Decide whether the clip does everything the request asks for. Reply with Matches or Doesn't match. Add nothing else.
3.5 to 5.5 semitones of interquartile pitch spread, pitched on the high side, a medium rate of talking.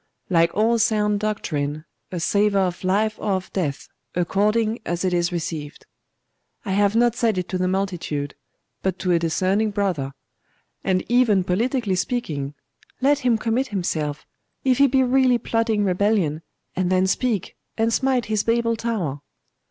Matches